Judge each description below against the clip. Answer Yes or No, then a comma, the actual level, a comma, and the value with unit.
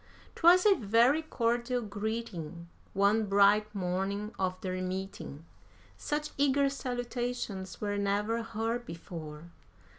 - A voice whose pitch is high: Yes, high, 210 Hz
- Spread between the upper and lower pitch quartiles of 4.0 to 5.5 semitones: Yes, average, 4.3 semitones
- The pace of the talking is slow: Yes, slow, 110 wpm